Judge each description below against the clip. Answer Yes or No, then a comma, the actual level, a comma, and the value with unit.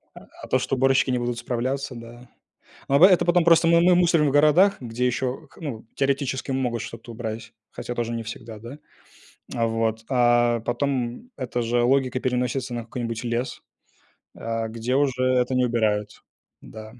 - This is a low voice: Yes, low, 125 Hz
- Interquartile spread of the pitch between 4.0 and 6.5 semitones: No, average, 2.7 semitones